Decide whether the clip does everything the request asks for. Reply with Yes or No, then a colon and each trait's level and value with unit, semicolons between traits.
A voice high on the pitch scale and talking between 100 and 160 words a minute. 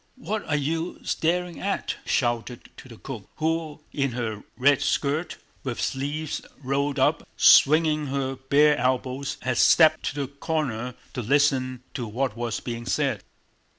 No: medium, 140 Hz; average, 150 wpm